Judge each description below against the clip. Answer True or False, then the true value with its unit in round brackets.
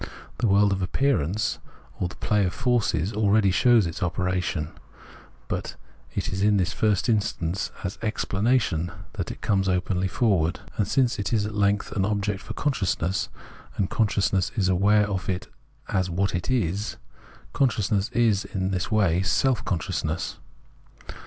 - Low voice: True (100 Hz)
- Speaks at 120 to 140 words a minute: False (155 wpm)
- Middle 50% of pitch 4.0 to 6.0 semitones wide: False (2.7 semitones)